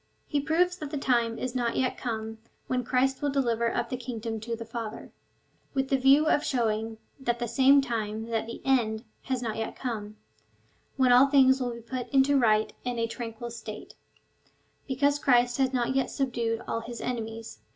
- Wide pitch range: No, average, 2.7 semitones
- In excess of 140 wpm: Yes, average, 190 wpm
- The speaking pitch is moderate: No, high, 240 Hz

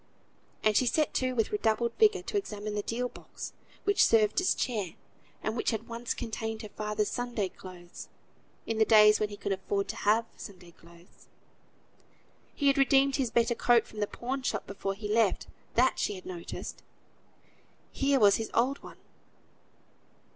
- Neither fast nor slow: Yes, average, 170 wpm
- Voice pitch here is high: Yes, high, 225 Hz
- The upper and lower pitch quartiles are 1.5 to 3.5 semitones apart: Yes, average, 3.2 semitones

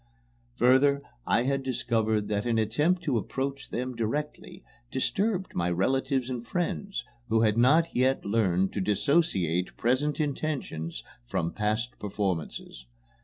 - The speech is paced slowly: Yes, slow, 125 wpm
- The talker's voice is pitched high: No, low, 125 Hz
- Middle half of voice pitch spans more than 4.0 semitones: Yes, average, 5.1 semitones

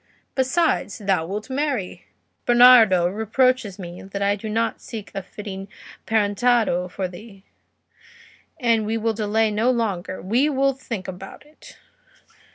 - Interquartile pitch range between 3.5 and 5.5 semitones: Yes, average, 3.9 semitones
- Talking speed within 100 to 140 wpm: Yes, slow, 135 wpm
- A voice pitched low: No, high, 215 Hz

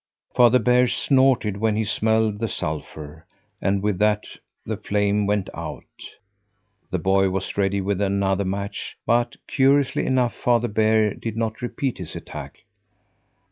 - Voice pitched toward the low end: Yes, low, 105 Hz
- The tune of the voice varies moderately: Yes, average, 3.1 semitones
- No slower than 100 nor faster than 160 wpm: Yes, average, 140 wpm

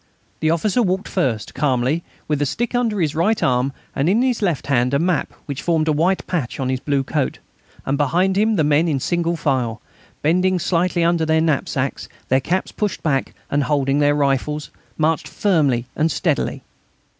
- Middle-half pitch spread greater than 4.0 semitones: Yes, average, 4.4 semitones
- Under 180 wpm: No, average, 185 wpm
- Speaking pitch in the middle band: Yes, medium, 155 Hz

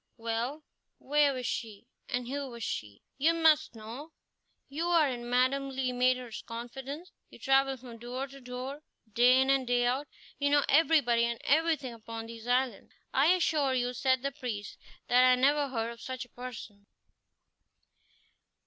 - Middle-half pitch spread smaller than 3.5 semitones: Yes, average, 2.7 semitones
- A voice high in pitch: Yes, very high, 255 Hz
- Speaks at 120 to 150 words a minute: No, average, 165 wpm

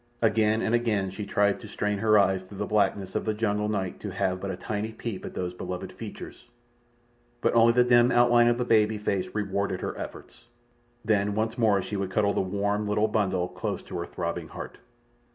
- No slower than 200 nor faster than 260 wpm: Yes, fast, 205 wpm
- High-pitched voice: No, low, 105 Hz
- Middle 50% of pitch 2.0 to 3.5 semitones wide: Yes, narrow, 2.4 semitones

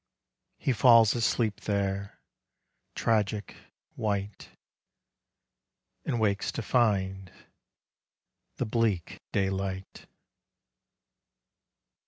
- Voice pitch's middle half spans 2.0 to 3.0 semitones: Yes, narrow, 2.5 semitones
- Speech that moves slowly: Yes, slow, 70 wpm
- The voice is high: No, low, 100 Hz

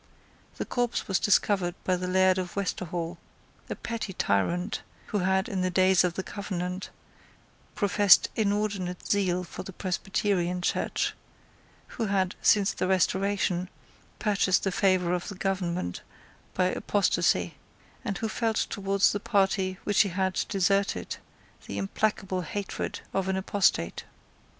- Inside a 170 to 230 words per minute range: No, slow, 135 wpm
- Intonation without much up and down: Yes, narrow, 1.8 semitones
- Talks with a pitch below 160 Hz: No, high, 190 Hz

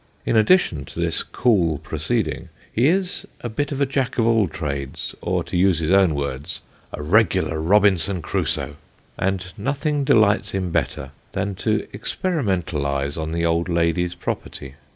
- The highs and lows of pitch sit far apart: Yes, wide, 5.7 semitones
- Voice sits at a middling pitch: No, very low, 90 Hz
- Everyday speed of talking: Yes, average, 165 wpm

